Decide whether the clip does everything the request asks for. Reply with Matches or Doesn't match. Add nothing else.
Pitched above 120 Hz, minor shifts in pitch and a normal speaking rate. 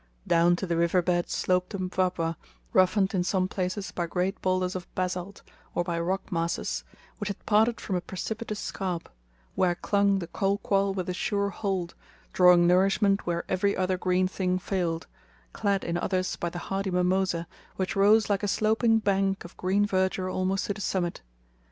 Matches